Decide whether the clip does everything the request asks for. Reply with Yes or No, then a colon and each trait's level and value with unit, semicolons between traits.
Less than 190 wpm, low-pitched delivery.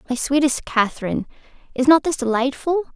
No: average, 140 wpm; very high, 270 Hz